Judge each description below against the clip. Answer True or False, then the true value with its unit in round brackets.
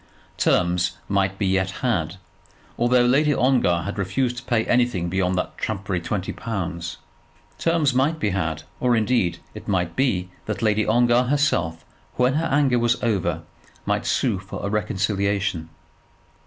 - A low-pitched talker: True (105 Hz)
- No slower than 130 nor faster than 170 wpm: True (150 wpm)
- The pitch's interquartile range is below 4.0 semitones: False (5.2 semitones)